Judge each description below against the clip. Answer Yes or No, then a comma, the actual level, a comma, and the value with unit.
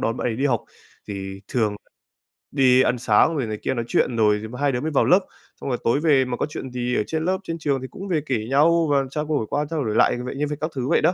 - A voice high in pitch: No, low, 135 Hz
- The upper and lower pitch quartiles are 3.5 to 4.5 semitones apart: Yes, average, 4.2 semitones